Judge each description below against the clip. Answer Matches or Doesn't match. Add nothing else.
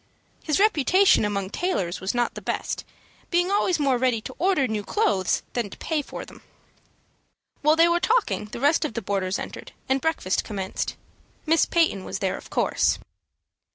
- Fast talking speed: Doesn't match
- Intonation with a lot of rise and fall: Matches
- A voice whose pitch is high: Matches